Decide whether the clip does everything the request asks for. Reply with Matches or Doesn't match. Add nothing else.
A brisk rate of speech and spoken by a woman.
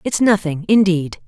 Doesn't match